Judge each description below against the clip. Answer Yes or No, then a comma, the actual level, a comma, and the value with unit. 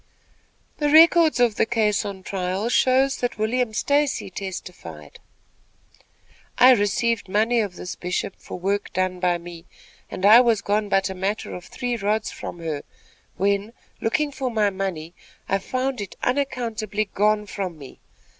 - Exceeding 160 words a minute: No, average, 155 wpm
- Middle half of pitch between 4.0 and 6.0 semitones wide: Yes, average, 4.3 semitones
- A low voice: No, high, 210 Hz